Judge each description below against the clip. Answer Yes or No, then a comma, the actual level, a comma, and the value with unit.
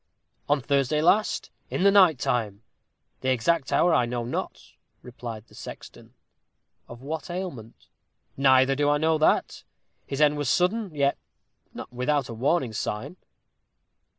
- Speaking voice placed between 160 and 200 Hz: No, medium, 140 Hz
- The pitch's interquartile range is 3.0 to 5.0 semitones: Yes, average, 4.6 semitones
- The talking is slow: No, average, 145 wpm